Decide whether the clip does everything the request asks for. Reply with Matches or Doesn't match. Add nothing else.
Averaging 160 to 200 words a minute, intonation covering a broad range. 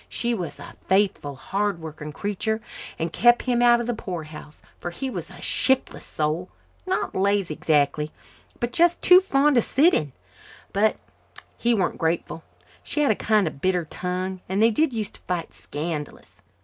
Matches